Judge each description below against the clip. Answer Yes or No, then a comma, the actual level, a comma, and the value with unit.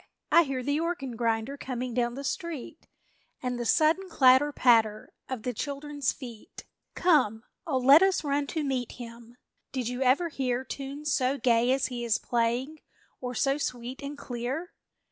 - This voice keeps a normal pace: Yes, average, 165 wpm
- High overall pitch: Yes, very high, 260 Hz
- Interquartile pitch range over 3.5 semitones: No, average, 3.0 semitones